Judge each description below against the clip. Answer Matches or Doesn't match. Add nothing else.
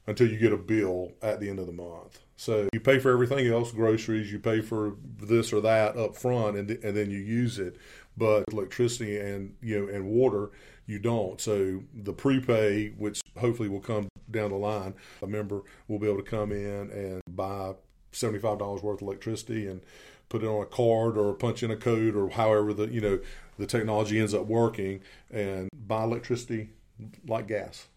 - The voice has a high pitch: Doesn't match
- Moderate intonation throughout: Doesn't match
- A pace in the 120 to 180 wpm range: Doesn't match